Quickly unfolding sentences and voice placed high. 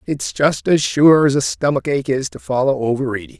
No: fast, 210 wpm; low, 120 Hz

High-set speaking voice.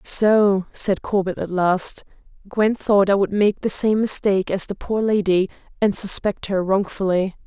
Yes: high, 195 Hz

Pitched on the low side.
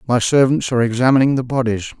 Yes: low, 125 Hz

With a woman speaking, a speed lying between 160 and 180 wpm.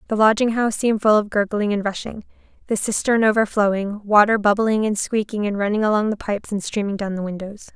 No: female; average, 200 wpm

